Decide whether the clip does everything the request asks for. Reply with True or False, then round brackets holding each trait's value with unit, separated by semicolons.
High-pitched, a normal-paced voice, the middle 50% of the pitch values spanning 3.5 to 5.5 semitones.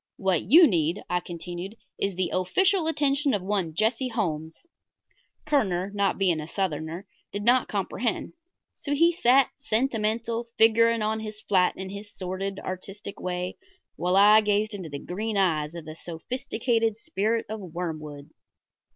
True (200 Hz; 150 wpm; 4.3 semitones)